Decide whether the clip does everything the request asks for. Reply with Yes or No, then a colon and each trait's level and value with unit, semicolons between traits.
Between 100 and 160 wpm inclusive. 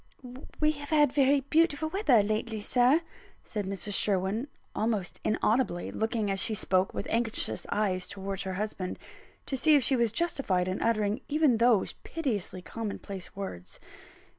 Yes: average, 155 wpm